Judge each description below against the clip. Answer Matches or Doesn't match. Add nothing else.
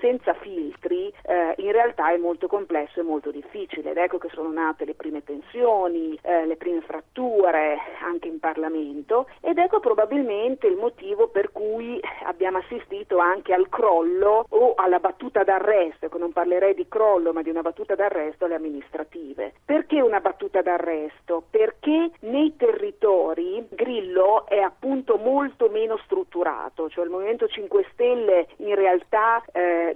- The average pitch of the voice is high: Matches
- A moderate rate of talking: Matches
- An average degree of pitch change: Doesn't match